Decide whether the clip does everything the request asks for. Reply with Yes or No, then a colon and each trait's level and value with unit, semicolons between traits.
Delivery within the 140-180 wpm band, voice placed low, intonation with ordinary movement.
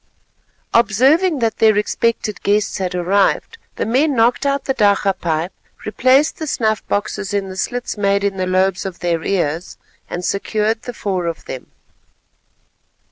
No: average, 155 wpm; high, 205 Hz; average, 3.9 semitones